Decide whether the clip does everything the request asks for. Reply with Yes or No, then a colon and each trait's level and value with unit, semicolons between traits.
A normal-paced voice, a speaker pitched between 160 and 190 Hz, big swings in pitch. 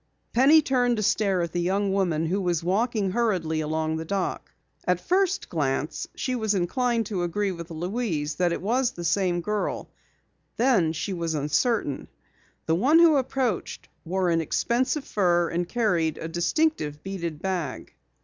Yes: average, 160 wpm; medium, 185 Hz; wide, 5.8 semitones